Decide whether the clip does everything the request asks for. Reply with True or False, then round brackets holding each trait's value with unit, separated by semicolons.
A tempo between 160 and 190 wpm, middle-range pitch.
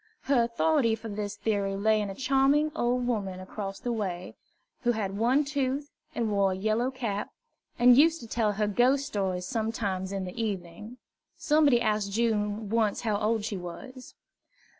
False (170 wpm; 220 Hz)